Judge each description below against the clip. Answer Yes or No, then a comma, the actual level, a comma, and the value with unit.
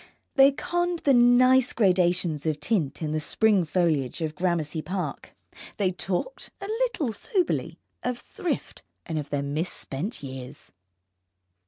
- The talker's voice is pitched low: No, medium, 180 Hz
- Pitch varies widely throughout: Yes, wide, 8.3 semitones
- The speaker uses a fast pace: No, slow, 135 wpm